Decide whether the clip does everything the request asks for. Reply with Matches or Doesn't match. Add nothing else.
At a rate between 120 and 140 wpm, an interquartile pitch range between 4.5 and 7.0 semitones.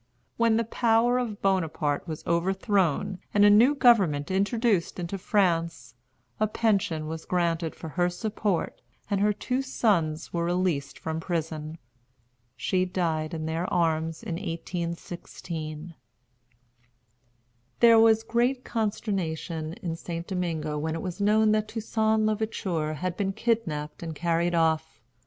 Matches